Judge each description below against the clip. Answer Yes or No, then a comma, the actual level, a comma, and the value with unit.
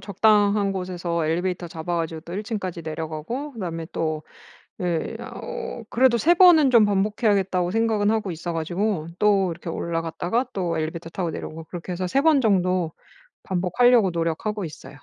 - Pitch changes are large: No, average, 4.4 semitones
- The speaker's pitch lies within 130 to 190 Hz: Yes, medium, 185 Hz